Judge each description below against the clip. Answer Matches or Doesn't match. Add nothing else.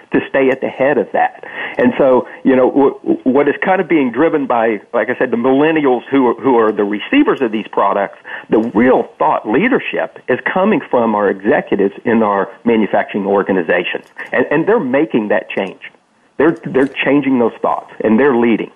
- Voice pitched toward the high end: Doesn't match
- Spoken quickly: Doesn't match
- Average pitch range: Doesn't match